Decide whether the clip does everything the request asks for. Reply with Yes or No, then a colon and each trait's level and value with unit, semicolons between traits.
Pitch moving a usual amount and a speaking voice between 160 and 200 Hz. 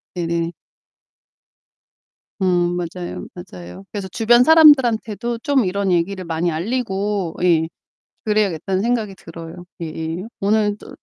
Yes: average, 4.4 semitones; high, 190 Hz